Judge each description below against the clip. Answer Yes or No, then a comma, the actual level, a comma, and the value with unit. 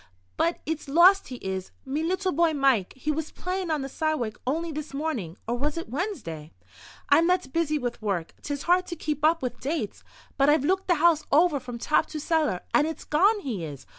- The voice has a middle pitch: No, very high, 300 Hz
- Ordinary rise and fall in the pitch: Yes, average, 4.9 semitones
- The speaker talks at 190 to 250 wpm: Yes, fast, 205 wpm